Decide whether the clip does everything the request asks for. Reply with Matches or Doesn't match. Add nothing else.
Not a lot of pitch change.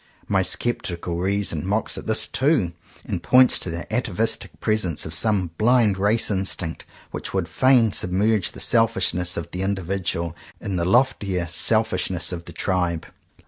Doesn't match